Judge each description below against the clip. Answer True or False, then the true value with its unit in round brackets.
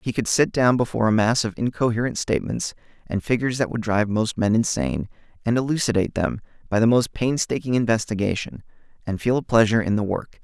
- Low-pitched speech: True (115 Hz)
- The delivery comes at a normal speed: True (190 wpm)